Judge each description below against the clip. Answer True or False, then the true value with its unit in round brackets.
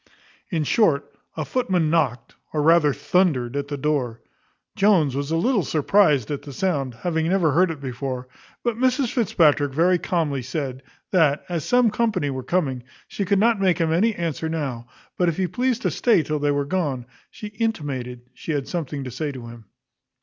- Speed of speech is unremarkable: True (185 wpm)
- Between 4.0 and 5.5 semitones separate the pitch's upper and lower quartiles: True (5.1 semitones)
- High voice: False (155 Hz)